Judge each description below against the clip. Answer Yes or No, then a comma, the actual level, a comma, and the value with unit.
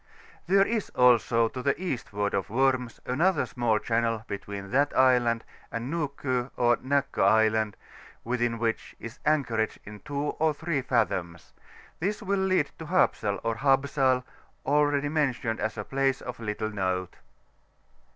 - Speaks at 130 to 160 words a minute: Yes, average, 140 wpm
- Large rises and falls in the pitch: No, average, 4.4 semitones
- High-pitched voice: No, low, 125 Hz